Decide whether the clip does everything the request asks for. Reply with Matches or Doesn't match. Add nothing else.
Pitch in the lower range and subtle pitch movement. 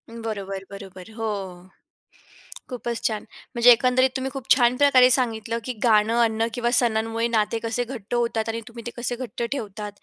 Doesn't match